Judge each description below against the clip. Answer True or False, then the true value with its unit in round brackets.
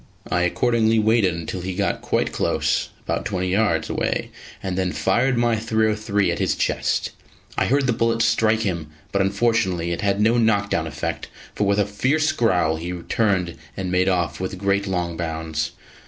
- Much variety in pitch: False (3.9 semitones)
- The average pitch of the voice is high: False (100 Hz)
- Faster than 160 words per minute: True (175 wpm)